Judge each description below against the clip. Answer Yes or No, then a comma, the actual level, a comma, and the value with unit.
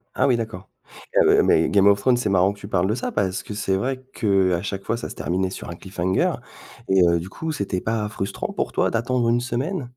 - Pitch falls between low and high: No, low, 100 Hz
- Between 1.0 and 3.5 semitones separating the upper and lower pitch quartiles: No, average, 4.0 semitones